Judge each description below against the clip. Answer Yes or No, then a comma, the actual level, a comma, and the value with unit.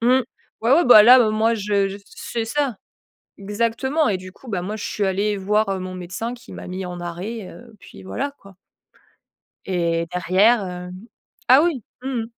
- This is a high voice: Yes, high, 210 Hz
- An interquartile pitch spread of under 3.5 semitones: No, average, 4.1 semitones